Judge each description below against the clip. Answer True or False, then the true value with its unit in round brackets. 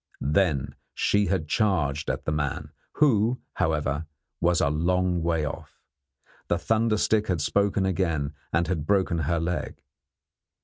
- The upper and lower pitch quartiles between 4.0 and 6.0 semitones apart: True (4.3 semitones)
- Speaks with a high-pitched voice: False (85 Hz)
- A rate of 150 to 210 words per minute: False (140 wpm)